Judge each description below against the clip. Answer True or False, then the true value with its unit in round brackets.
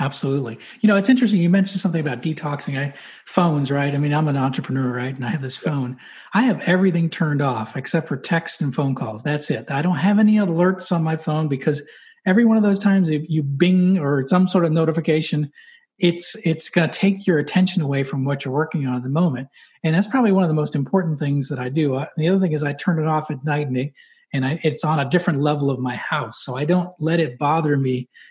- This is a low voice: False (155 Hz)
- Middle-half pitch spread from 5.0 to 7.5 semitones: False (4.2 semitones)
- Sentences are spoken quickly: True (245 wpm)